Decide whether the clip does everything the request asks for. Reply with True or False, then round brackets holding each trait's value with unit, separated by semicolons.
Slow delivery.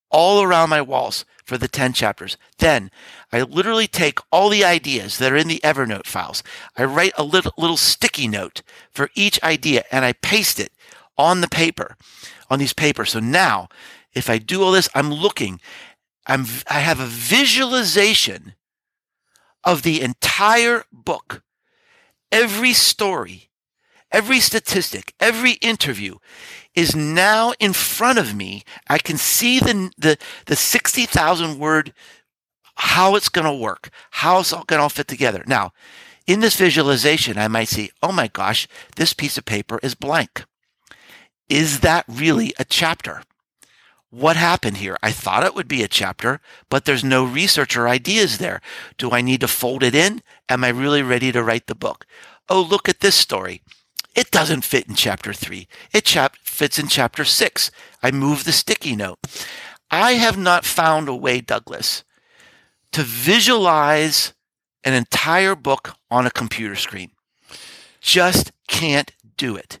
False (160 wpm)